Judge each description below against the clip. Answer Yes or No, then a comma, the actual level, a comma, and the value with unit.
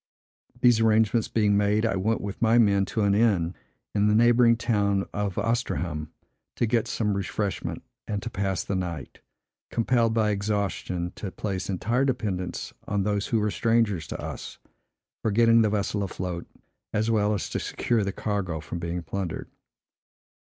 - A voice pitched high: No, low, 105 Hz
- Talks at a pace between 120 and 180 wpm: Yes, average, 165 wpm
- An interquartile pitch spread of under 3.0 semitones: Yes, narrow, 2.6 semitones